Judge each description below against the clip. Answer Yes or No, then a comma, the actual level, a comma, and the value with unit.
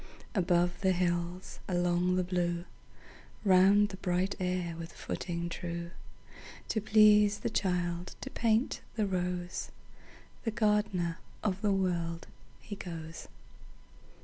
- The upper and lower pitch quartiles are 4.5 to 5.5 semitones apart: No, narrow, 2.6 semitones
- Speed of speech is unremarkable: No, slow, 105 wpm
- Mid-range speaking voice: Yes, medium, 180 Hz